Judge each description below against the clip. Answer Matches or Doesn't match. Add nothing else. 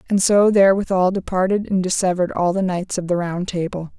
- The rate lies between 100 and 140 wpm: Doesn't match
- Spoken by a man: Doesn't match